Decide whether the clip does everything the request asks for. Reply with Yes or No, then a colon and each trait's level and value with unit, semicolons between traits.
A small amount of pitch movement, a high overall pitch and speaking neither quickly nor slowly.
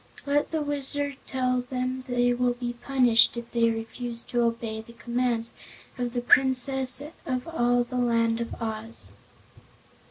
Yes: narrow, 1.7 semitones; high, 245 Hz; average, 150 wpm